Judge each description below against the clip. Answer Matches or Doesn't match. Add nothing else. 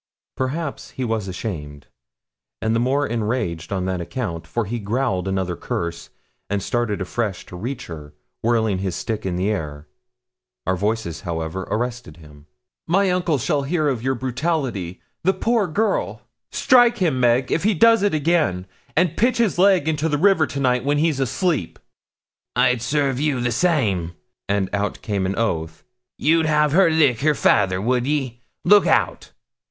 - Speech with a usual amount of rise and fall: Doesn't match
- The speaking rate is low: Doesn't match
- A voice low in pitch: Matches